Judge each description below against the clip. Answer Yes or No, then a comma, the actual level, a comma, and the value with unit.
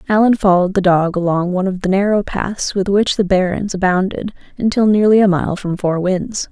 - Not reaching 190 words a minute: No, fast, 205 wpm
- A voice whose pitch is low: No, high, 190 Hz